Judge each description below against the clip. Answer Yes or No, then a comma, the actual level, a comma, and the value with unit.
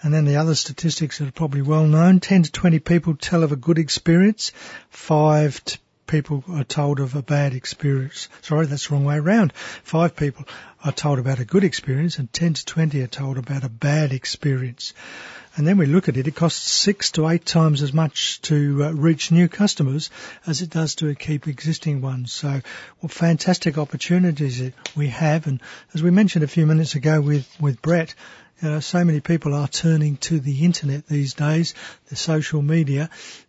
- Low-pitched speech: No, medium, 155 Hz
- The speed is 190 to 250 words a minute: Yes, average, 195 wpm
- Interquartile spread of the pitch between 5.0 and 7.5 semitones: No, narrow, 2.6 semitones